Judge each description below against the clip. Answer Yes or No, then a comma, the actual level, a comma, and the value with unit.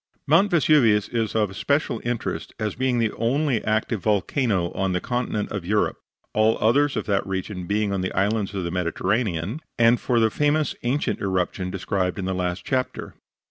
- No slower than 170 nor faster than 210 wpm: Yes, average, 180 wpm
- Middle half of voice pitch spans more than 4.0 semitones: Yes, average, 4.4 semitones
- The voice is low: Yes, low, 110 Hz